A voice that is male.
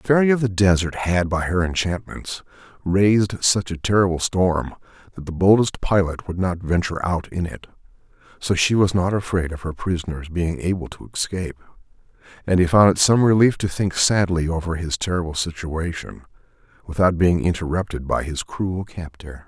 Yes: male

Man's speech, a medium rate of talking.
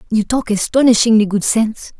No: female; average, 150 wpm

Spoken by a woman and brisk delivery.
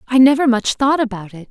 Yes: female; fast, 240 wpm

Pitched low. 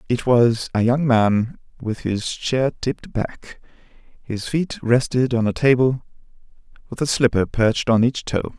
Yes: low, 120 Hz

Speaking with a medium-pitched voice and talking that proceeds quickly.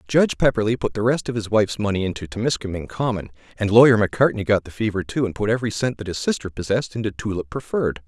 No: low, 110 Hz; fast, 225 wpm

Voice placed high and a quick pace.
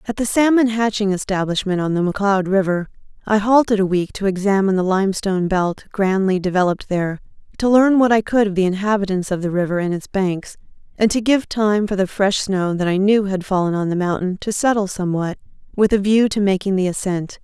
Yes: high, 195 Hz; fast, 210 wpm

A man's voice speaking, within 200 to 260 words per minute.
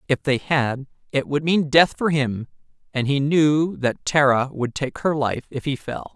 Yes: male; fast, 205 wpm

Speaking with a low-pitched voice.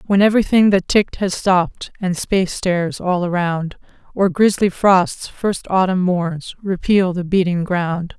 No: medium, 185 Hz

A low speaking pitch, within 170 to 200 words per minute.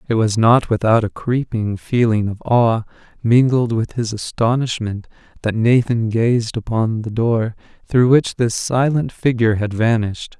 No: low, 115 Hz; average, 150 wpm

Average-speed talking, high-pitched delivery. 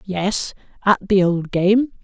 Yes: average, 150 wpm; high, 195 Hz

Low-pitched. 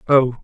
Yes: low, 130 Hz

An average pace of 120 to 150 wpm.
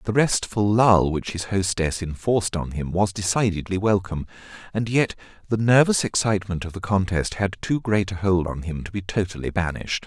No: average, 185 wpm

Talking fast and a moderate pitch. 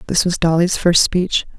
No: average, 190 wpm; medium, 175 Hz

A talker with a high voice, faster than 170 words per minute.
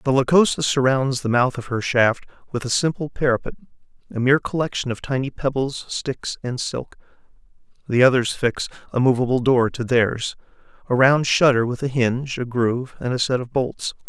No: low, 130 Hz; average, 180 wpm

